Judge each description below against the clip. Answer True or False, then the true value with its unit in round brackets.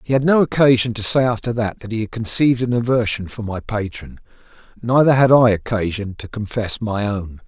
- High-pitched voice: False (115 Hz)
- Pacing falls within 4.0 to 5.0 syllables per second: False (5.5 syllables/s)